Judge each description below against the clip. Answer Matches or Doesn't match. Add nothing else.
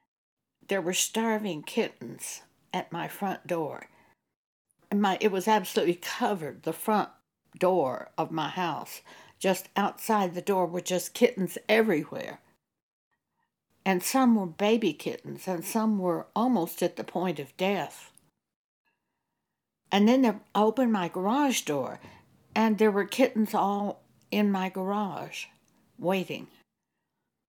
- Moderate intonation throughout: Matches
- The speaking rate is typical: Doesn't match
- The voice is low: Doesn't match